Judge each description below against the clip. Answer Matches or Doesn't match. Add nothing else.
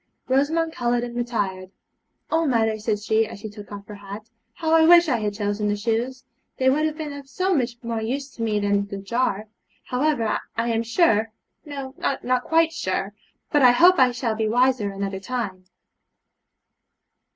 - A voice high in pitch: Matches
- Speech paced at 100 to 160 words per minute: Doesn't match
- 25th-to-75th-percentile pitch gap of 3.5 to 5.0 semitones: Matches